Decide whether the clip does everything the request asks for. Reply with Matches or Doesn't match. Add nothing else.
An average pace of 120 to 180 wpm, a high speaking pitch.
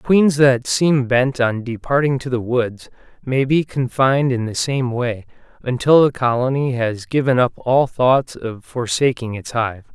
Doesn't match